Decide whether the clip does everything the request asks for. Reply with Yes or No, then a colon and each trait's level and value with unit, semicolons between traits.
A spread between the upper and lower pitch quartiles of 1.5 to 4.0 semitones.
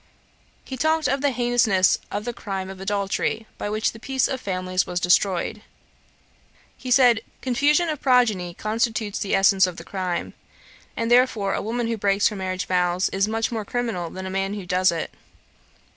No: average, 4.4 semitones